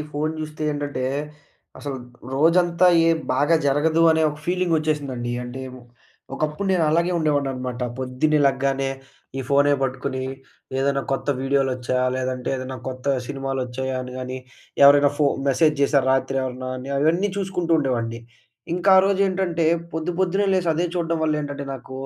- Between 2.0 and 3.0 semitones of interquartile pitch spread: No, average, 3.7 semitones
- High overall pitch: No, medium, 140 Hz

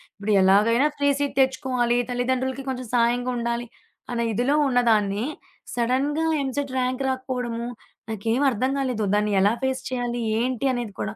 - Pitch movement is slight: Yes, narrow, 2.1 semitones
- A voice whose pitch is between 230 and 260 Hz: Yes, high, 245 Hz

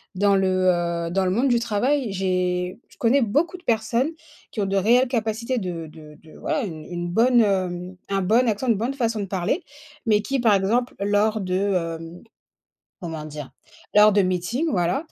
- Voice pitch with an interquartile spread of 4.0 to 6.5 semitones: Yes, average, 4.6 semitones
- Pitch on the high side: Yes, high, 205 Hz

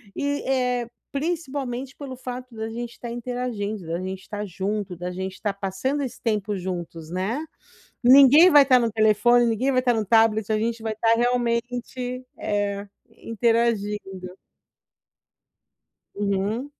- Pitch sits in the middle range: No, high, 230 Hz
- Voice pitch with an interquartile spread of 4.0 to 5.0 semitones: No, average, 3.6 semitones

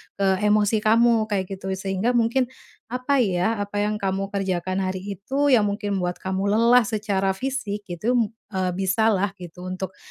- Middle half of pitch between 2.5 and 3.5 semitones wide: Yes, average, 2.9 semitones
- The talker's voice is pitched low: No, high, 200 Hz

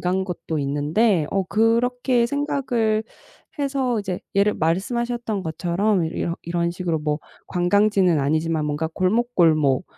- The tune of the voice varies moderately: No, wide, 5.8 semitones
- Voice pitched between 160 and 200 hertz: Yes, medium, 185 Hz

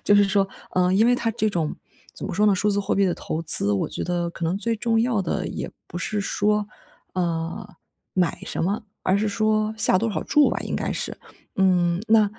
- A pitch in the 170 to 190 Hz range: No, high, 200 Hz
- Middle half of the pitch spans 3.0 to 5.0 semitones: Yes, average, 3.3 semitones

